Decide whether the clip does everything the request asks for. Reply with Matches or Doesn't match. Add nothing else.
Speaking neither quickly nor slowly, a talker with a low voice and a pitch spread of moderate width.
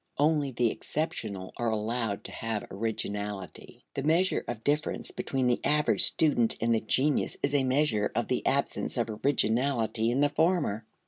Matches